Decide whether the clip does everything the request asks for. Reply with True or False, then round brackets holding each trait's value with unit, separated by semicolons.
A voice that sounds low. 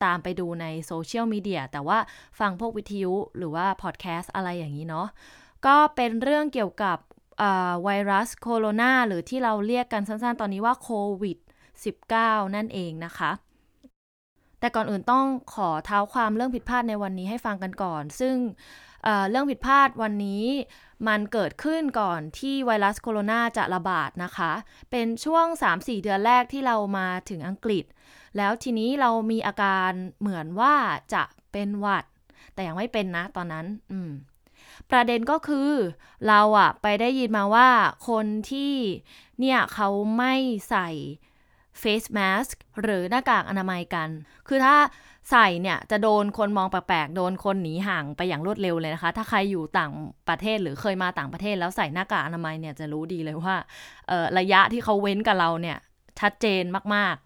False (205 Hz)